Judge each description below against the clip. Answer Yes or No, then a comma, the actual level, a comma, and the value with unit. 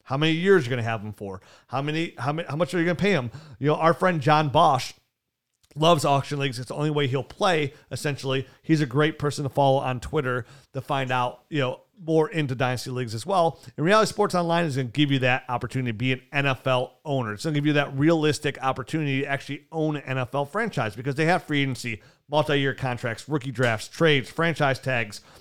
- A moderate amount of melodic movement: Yes, average, 3.2 semitones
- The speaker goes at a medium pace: No, fast, 235 wpm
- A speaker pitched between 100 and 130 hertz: No, medium, 140 Hz